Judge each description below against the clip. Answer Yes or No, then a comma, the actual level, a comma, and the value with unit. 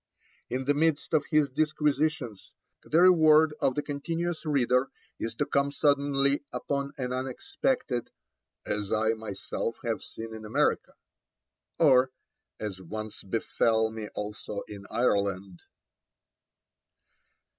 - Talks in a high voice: No, low, 130 Hz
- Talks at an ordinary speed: No, slow, 115 wpm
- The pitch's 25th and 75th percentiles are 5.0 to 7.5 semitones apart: Yes, average, 5.3 semitones